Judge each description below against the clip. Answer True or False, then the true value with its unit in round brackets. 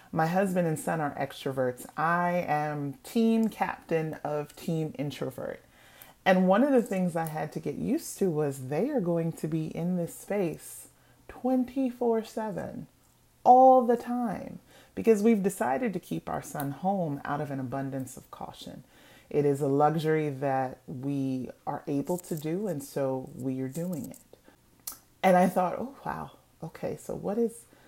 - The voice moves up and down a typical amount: False (7.1 semitones)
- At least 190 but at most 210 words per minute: False (165 wpm)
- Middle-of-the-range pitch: True (165 Hz)